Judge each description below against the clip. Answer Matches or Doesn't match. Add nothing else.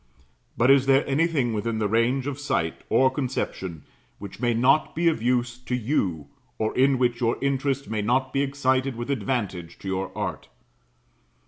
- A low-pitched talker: Matches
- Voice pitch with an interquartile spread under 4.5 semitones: Matches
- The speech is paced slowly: Doesn't match